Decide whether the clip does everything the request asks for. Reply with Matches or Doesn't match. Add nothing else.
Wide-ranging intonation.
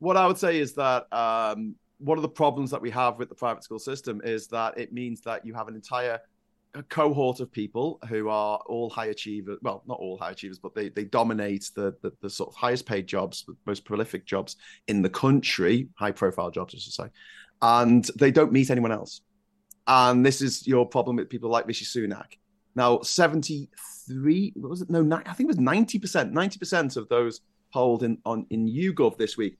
Matches